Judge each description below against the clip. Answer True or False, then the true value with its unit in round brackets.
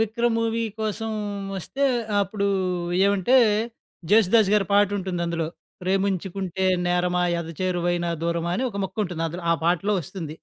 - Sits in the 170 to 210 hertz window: True (190 Hz)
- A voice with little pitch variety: False (3.1 semitones)